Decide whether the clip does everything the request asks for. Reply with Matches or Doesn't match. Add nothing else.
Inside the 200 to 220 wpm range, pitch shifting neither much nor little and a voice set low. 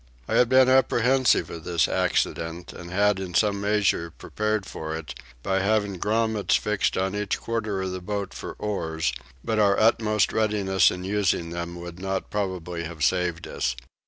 Doesn't match